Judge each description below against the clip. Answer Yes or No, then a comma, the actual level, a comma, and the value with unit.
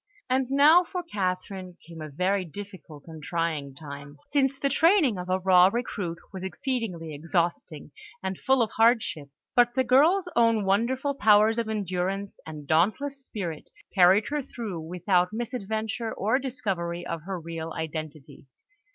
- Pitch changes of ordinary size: No, wide, 6.2 semitones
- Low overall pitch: No, high, 195 Hz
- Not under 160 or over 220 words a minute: No, average, 150 wpm